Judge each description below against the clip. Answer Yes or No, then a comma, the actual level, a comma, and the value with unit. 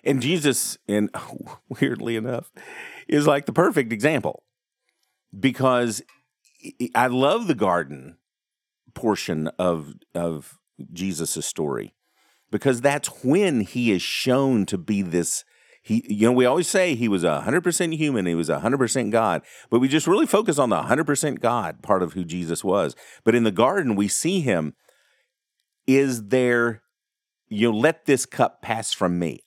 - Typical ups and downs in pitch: No, wide, 6.4 semitones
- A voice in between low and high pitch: No, low, 115 Hz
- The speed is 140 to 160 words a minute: Yes, average, 150 wpm